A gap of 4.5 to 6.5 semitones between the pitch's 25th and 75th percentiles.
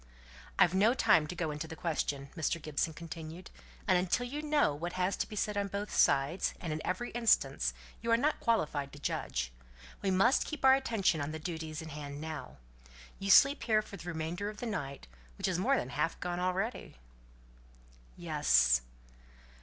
Yes: wide, 5.6 semitones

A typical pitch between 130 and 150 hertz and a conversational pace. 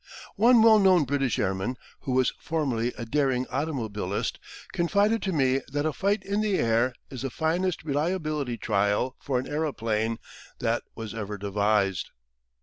Yes: low, 135 Hz; average, 150 wpm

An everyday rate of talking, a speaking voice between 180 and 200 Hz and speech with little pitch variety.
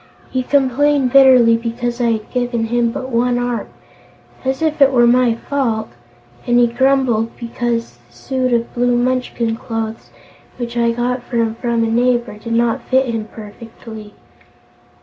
No: average, 160 wpm; high, 240 Hz; narrow, 1.7 semitones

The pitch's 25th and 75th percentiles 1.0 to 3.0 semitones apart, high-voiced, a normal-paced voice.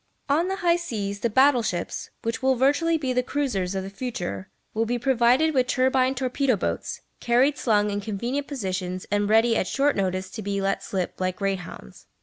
No: average, 5.2 semitones; high, 235 Hz; average, 190 wpm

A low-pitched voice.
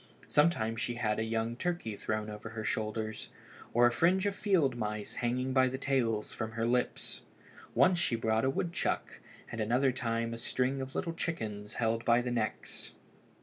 Yes: low, 120 Hz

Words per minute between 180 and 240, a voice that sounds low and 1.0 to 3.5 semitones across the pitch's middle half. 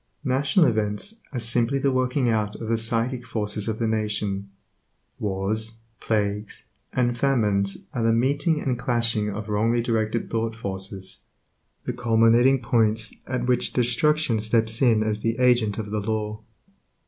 No: average, 150 wpm; low, 115 Hz; narrow, 2.4 semitones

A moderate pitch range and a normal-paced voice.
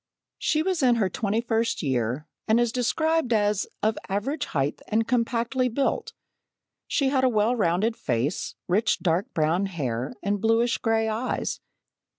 Yes: average, 4.6 semitones; average, 155 wpm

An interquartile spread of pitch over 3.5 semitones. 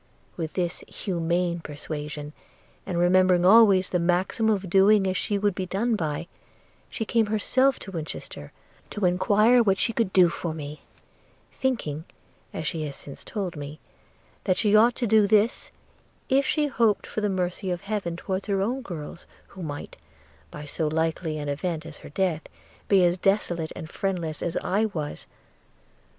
Yes: average, 4.3 semitones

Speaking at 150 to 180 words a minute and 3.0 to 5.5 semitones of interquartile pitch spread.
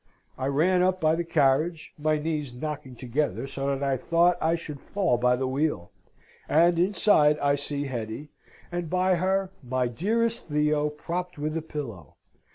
Yes: average, 165 wpm; average, 4.1 semitones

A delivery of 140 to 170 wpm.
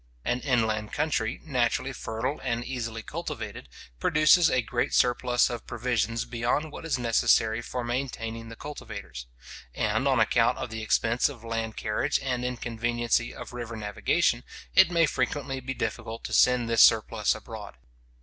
Yes: average, 150 wpm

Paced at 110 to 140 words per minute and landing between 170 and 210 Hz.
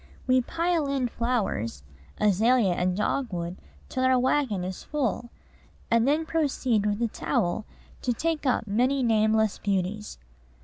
No: slow, 135 wpm; high, 230 Hz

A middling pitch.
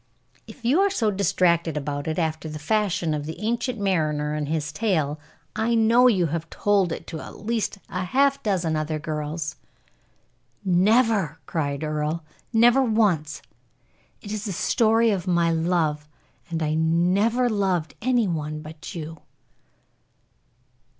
Yes: medium, 170 Hz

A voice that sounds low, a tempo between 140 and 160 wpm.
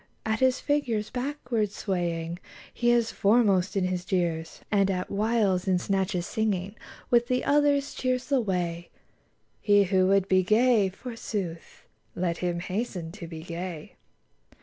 No: high, 195 Hz; average, 145 wpm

